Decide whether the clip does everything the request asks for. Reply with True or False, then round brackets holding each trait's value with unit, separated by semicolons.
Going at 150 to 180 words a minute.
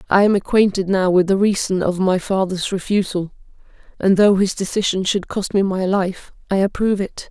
False (190 wpm)